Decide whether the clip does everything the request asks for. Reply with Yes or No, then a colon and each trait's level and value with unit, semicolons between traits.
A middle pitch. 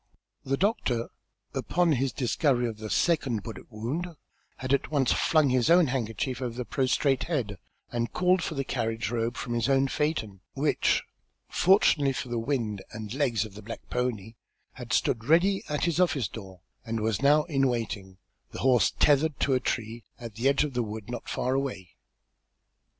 No: low, 125 Hz